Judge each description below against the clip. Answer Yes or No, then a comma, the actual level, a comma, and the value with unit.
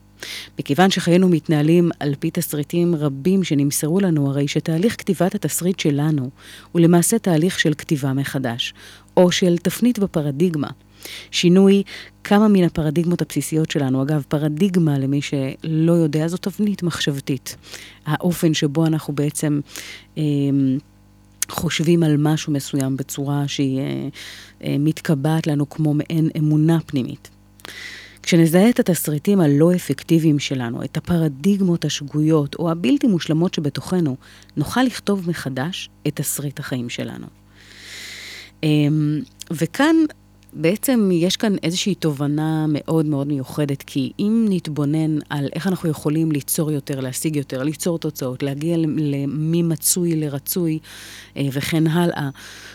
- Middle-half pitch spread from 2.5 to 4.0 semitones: Yes, average, 3.4 semitones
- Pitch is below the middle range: No, medium, 155 Hz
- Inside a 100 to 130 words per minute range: Yes, average, 120 wpm